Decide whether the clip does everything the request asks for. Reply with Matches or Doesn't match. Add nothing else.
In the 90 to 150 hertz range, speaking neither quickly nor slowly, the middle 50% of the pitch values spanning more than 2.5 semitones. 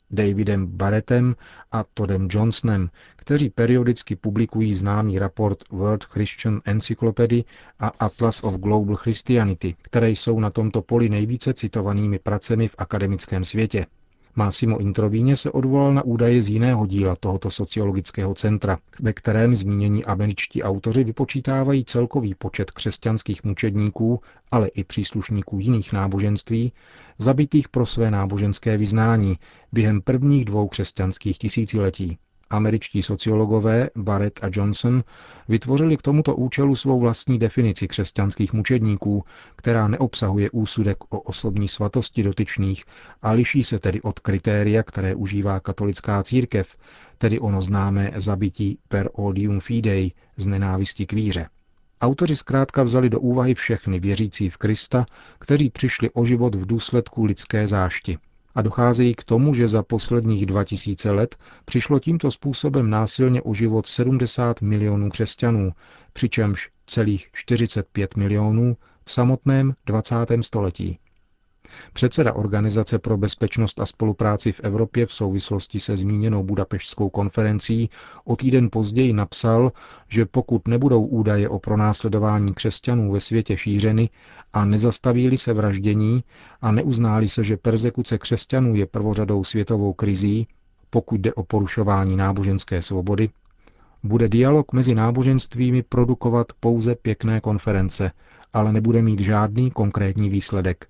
Matches